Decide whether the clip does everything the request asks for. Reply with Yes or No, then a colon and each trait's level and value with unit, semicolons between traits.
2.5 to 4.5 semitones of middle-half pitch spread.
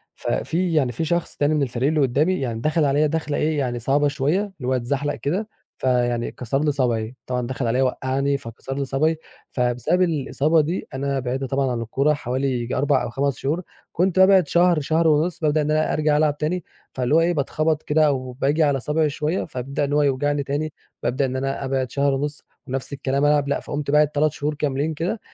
Yes: average, 2.8 semitones